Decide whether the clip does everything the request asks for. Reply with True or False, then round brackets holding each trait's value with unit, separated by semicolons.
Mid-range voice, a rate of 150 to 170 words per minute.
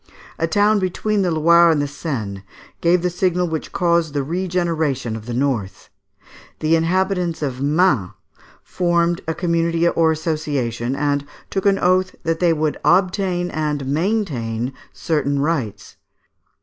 False (165 Hz; 140 wpm)